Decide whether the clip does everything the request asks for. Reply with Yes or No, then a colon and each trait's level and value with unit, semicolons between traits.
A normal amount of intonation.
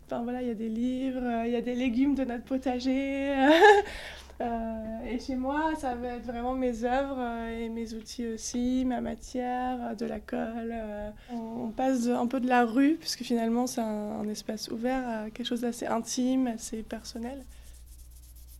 No: narrow, 2.0 semitones